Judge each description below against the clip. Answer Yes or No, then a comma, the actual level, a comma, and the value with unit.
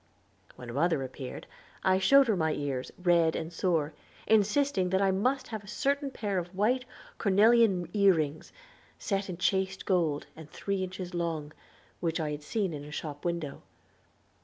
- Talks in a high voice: No, medium, 180 Hz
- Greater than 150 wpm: Yes, average, 165 wpm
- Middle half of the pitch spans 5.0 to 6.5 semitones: No, average, 4.1 semitones